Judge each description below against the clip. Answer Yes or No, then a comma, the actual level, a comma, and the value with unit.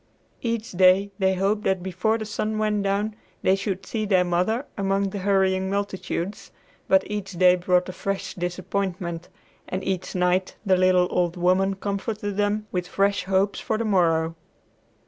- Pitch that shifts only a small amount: Yes, narrow, 1.9 semitones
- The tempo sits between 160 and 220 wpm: Yes, average, 165 wpm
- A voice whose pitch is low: No, high, 190 Hz